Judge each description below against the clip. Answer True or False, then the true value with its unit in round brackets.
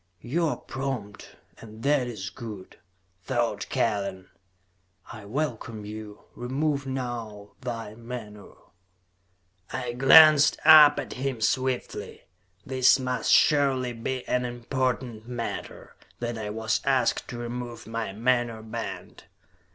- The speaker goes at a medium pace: False (115 wpm)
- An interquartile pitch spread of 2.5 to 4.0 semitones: True (3.1 semitones)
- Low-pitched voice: True (120 Hz)